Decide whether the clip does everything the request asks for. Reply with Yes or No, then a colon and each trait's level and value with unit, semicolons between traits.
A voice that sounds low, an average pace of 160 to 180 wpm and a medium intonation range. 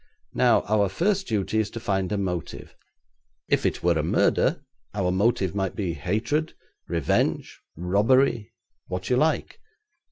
No: low, 100 Hz; average, 140 wpm; average, 4.1 semitones